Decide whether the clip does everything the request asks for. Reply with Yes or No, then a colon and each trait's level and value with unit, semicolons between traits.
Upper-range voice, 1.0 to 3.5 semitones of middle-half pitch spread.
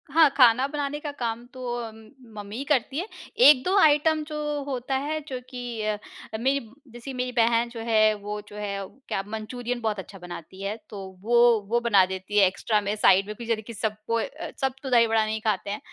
No: high, 235 Hz; average, 4.1 semitones